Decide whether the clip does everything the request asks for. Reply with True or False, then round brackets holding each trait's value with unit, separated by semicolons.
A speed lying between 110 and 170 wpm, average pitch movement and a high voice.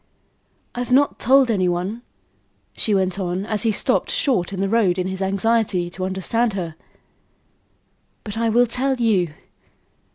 True (155 wpm; 3.9 semitones; 205 Hz)